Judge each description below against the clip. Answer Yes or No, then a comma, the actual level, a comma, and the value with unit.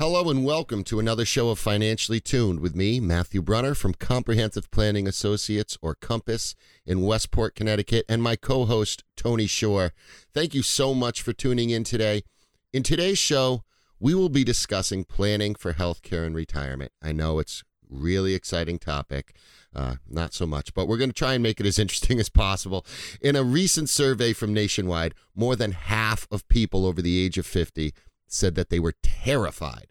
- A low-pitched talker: Yes, low, 105 Hz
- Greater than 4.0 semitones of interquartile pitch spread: Yes, average, 5.1 semitones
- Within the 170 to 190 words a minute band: Yes, average, 185 wpm